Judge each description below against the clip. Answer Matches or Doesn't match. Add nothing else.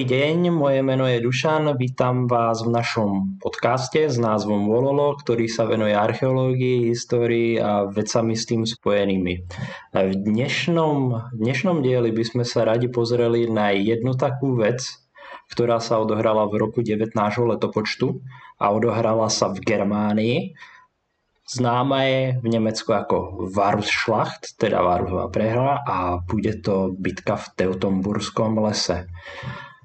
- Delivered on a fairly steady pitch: Doesn't match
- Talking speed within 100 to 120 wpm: Doesn't match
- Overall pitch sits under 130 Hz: Matches